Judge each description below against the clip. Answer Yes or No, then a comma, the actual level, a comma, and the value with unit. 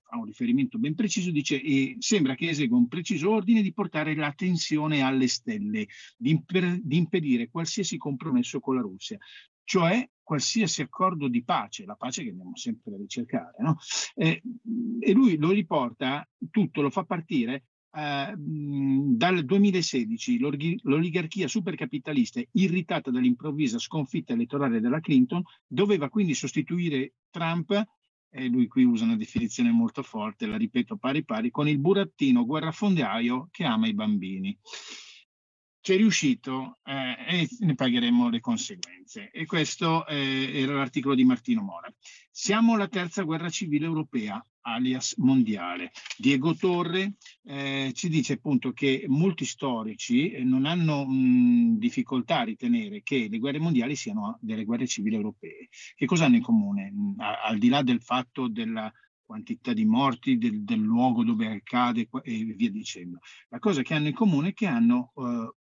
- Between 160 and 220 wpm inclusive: No, average, 150 wpm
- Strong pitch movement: Yes, wide, 8.0 semitones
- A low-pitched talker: No, high, 195 Hz